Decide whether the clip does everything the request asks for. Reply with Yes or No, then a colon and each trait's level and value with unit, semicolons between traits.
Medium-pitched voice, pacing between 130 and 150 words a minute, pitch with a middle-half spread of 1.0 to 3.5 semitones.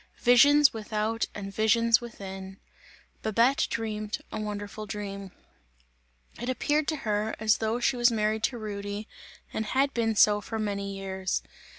No: high, 215 Hz; average, 145 wpm; narrow, 2.4 semitones